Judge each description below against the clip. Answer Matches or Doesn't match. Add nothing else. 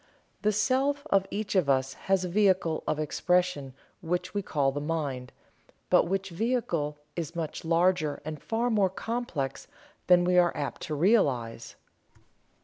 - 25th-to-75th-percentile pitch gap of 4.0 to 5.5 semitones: Matches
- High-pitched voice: Doesn't match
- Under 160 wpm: Matches